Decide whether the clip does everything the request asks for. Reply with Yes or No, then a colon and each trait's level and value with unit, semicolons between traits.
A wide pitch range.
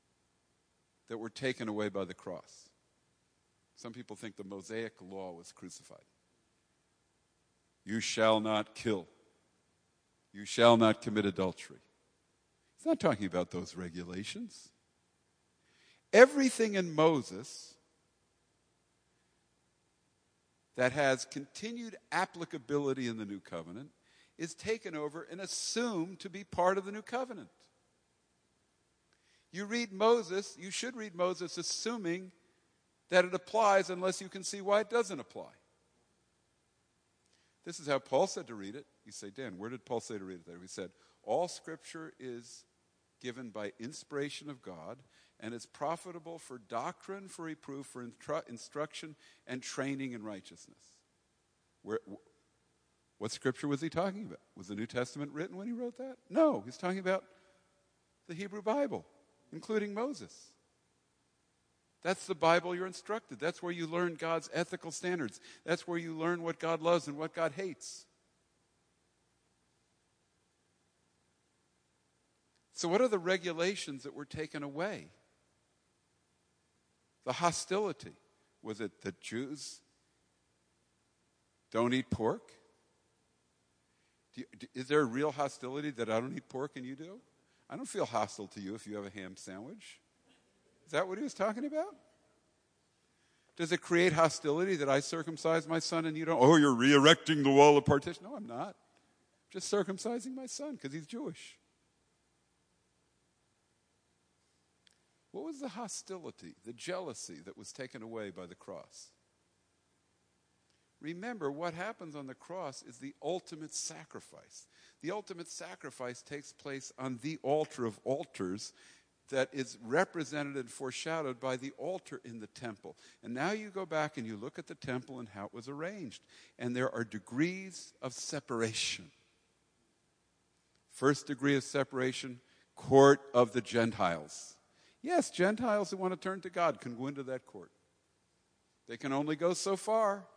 Yes: wide, 7.1 semitones